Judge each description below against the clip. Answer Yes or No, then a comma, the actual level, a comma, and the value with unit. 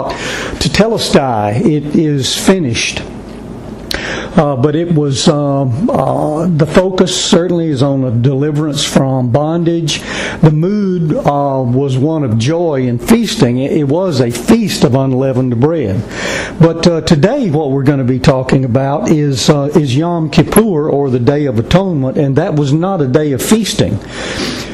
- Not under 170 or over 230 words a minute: No, average, 155 wpm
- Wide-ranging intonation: No, average, 4.0 semitones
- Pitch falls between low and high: Yes, medium, 150 Hz